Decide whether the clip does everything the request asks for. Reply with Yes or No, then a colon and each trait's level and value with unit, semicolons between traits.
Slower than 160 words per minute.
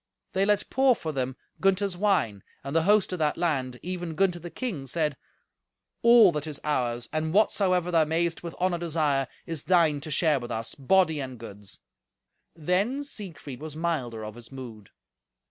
No: average, 175 wpm